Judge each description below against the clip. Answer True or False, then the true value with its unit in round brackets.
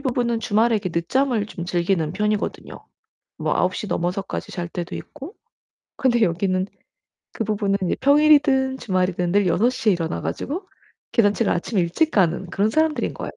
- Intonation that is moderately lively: False (5.9 semitones)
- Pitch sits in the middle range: False (205 Hz)